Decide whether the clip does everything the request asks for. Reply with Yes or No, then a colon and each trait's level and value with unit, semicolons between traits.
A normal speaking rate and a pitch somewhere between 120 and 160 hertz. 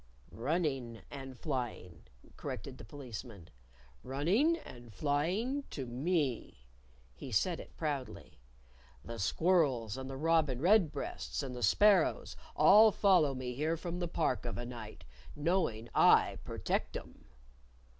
No: slow, 130 wpm; medium, 140 Hz